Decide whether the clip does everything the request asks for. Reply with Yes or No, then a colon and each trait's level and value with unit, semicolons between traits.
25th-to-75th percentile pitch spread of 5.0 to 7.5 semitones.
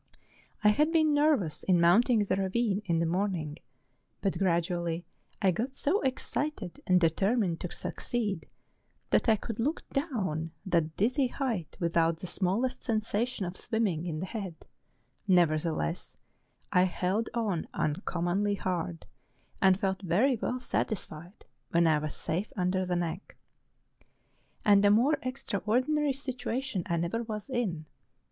Yes: wide, 5.6 semitones